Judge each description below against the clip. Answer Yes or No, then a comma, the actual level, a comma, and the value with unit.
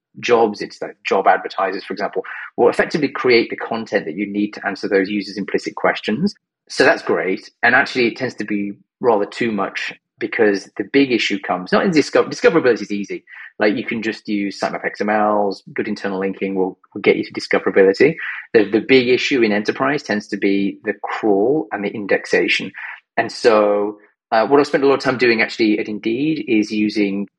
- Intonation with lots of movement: No, average, 3.7 semitones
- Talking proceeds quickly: No, average, 195 wpm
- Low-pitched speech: Yes, low, 105 Hz